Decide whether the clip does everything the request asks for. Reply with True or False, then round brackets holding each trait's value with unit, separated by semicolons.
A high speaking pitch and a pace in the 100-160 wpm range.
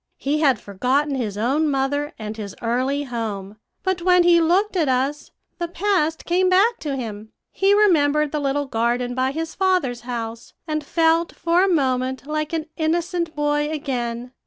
False (290 Hz; 170 wpm)